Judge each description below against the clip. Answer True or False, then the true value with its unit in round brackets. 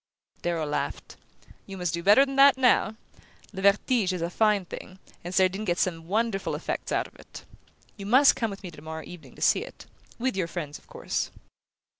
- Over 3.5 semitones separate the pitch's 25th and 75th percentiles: True (4.2 semitones)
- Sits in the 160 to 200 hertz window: True (190 Hz)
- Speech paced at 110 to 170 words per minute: False (195 wpm)